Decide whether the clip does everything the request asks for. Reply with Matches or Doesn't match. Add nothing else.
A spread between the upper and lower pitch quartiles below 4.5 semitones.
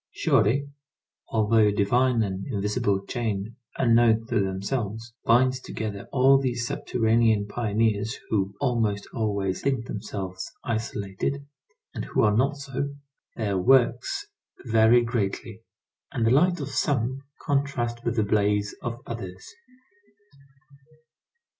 Matches